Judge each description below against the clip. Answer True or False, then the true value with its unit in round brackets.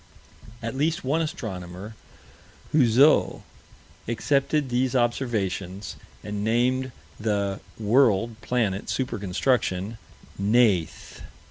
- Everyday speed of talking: False (85 wpm)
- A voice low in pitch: True (115 Hz)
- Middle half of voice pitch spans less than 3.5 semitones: False (4.4 semitones)